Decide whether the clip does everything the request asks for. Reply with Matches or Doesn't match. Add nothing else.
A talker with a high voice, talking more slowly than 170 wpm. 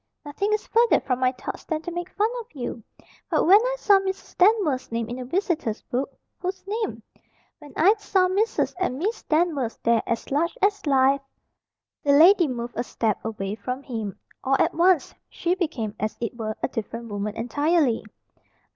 Doesn't match